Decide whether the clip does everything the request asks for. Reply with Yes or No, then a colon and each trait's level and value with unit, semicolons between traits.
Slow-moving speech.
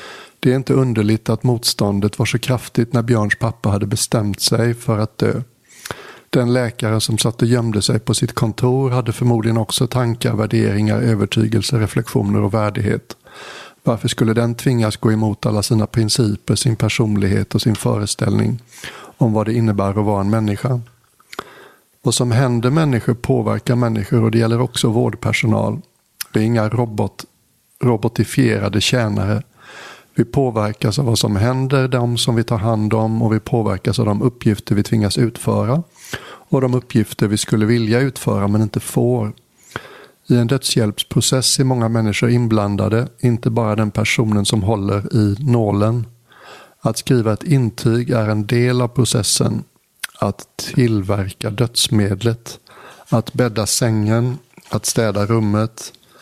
No: average, 150 wpm